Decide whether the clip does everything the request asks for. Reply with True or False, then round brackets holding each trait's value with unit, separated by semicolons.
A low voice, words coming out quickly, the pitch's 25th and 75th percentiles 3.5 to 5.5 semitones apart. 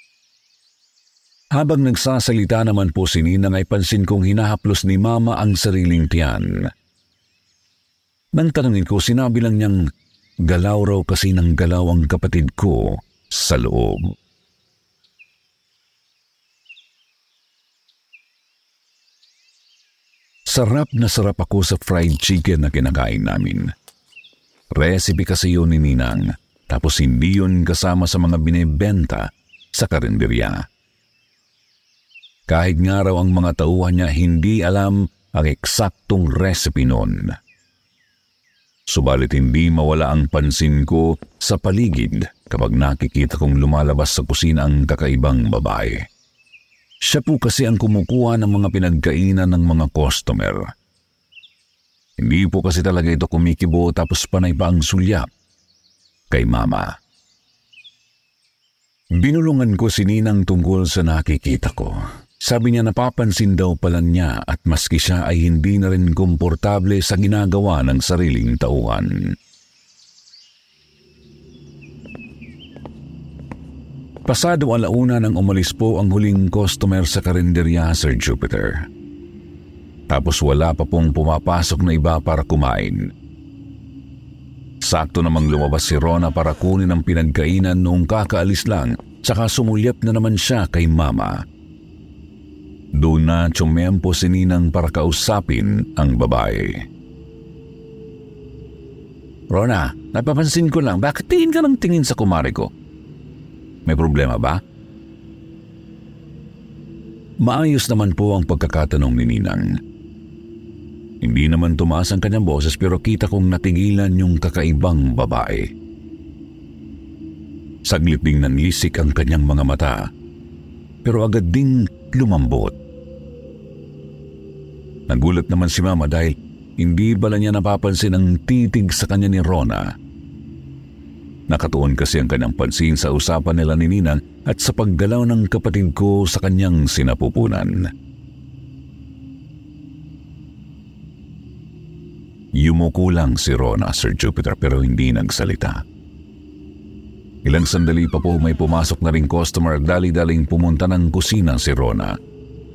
False (85 Hz; 115 wpm; 4.3 semitones)